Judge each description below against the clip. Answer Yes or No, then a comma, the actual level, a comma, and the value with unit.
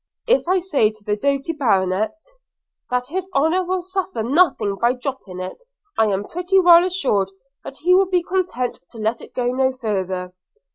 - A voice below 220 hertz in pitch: No, very high, 265 Hz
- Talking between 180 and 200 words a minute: Yes, average, 185 wpm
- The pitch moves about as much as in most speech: No, wide, 8.9 semitones